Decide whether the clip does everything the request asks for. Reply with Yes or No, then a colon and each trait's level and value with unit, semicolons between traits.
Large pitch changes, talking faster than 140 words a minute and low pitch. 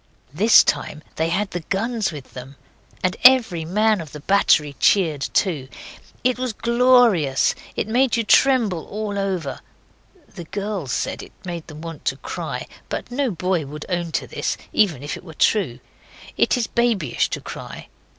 No: wide, 6.0 semitones; average, 170 wpm; high, 190 Hz